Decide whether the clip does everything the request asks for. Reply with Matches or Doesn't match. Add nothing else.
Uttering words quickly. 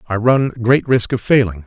Matches